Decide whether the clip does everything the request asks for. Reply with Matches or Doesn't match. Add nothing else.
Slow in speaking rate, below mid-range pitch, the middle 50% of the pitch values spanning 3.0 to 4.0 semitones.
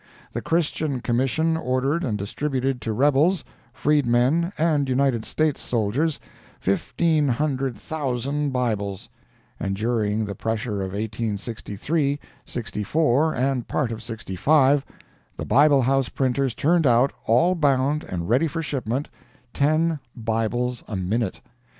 Doesn't match